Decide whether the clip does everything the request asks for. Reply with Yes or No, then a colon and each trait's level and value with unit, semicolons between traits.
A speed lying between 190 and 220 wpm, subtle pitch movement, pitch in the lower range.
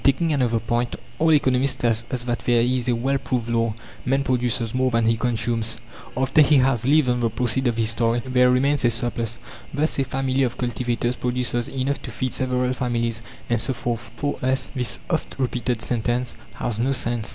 Yes: average, 195 wpm; narrow, 1.9 semitones; low, 125 Hz